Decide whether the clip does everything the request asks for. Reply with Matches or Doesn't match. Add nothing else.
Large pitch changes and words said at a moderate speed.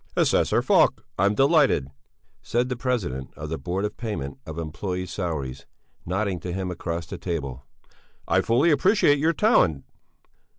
Matches